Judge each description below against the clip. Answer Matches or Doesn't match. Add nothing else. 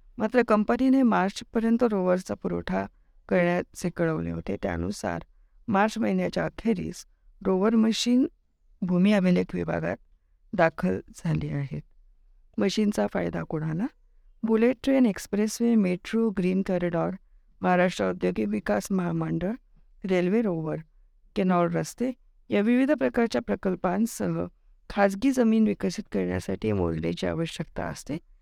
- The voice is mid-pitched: Matches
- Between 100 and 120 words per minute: Matches